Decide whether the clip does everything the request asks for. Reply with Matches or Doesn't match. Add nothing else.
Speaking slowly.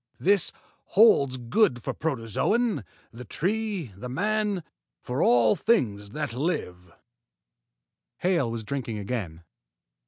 Matches